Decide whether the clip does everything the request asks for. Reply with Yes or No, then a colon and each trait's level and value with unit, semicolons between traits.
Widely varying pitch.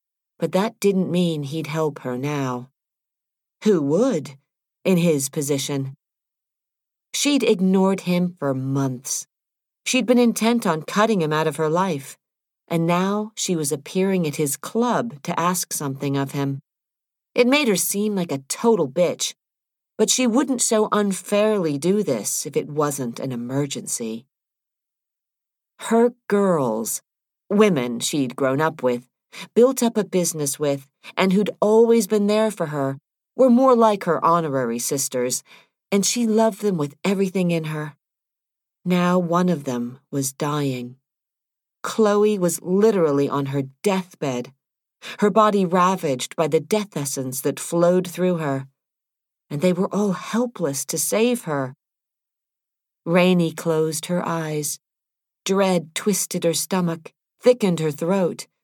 Yes: wide, 6.1 semitones